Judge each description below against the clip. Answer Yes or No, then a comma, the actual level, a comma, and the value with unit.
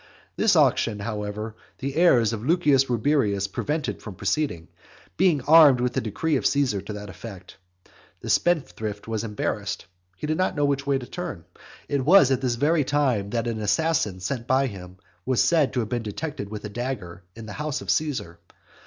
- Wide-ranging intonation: Yes, wide, 5.8 semitones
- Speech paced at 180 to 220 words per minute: Yes, average, 190 wpm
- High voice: No, low, 125 Hz